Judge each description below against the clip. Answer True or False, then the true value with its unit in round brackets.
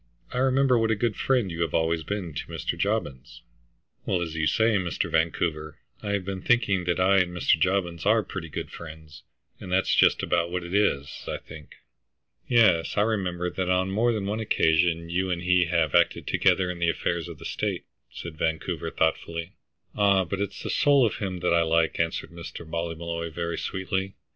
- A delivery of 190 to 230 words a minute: True (195 wpm)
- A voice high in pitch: False (90 Hz)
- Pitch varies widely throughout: False (3.0 semitones)